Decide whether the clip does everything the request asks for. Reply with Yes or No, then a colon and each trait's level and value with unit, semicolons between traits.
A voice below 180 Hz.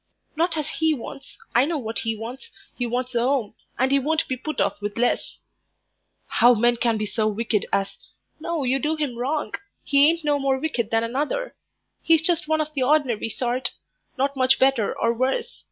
No: very high, 265 Hz